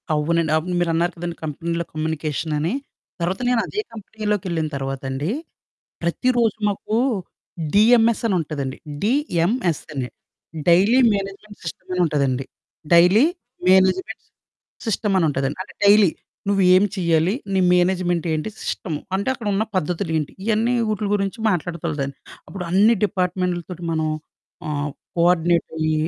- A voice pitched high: No, medium, 180 Hz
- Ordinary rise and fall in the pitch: Yes, average, 4.2 semitones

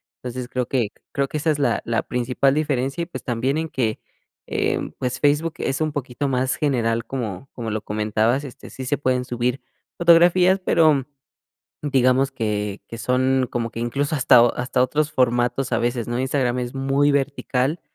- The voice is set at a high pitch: No, low, 130 Hz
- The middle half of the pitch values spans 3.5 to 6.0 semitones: No, average, 2.9 semitones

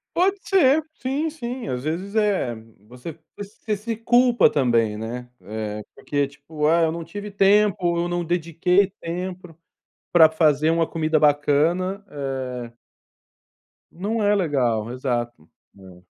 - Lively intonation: Yes, wide, 7.2 semitones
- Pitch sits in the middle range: Yes, medium, 165 Hz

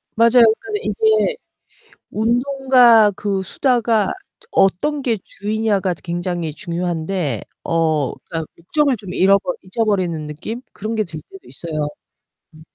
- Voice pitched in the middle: No, high, 200 Hz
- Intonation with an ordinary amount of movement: No, wide, 5.8 semitones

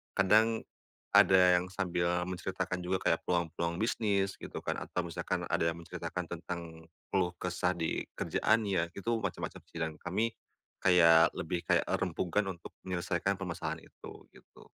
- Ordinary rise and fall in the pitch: No, narrow, 2.1 semitones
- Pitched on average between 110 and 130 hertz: No, very low, 90 Hz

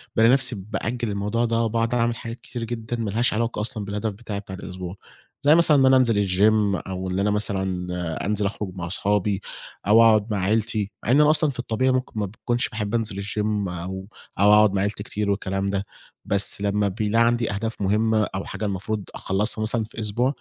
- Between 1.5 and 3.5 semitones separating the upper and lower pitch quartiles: Yes, narrow, 2.6 semitones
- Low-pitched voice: Yes, low, 105 Hz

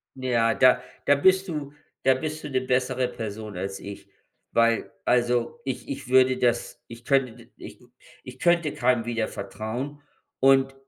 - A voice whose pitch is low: Yes, low, 130 Hz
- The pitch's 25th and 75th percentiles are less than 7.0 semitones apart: Yes, narrow, 2.6 semitones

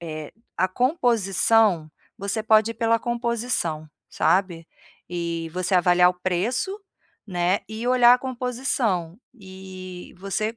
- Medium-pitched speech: No, high, 195 Hz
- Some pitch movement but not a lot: Yes, average, 4.8 semitones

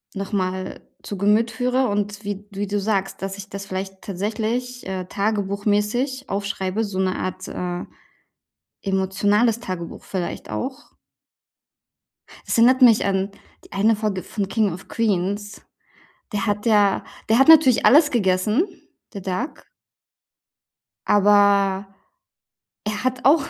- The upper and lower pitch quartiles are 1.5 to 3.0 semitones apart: Yes, narrow, 2.6 semitones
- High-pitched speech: Yes, high, 205 Hz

